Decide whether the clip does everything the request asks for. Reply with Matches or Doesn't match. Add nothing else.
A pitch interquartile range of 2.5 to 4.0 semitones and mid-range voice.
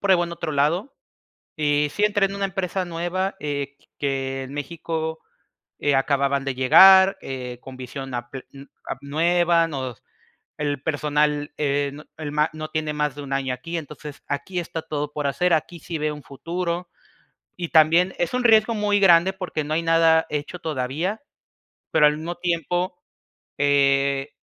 Matches